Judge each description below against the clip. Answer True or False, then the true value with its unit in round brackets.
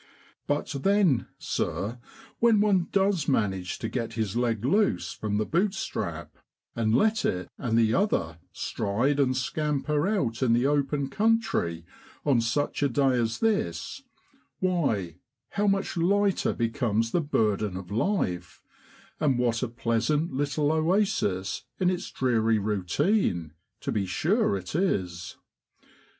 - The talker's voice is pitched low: True (130 Hz)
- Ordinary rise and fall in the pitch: False (8.3 semitones)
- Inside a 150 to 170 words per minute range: False (135 wpm)